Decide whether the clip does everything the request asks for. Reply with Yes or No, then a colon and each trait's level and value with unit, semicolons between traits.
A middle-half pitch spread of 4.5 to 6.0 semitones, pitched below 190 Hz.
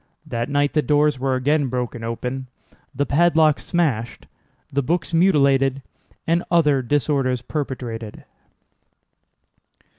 No: average, 3.1 semitones; medium, 140 Hz